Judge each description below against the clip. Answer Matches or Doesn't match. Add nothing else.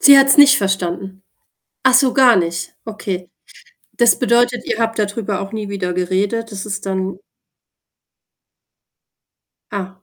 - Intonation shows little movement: Doesn't match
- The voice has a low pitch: Doesn't match